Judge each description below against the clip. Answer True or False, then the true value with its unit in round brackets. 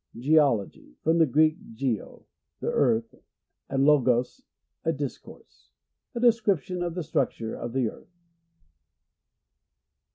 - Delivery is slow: True (120 wpm)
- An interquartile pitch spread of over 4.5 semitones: True (5.6 semitones)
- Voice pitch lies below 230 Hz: True (140 Hz)